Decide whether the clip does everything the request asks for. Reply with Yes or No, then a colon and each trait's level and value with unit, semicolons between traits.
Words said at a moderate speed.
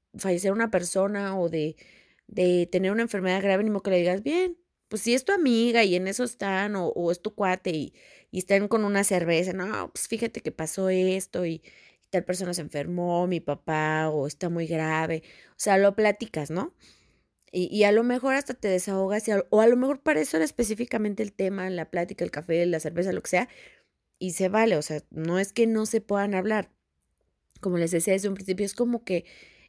No: fast, 220 wpm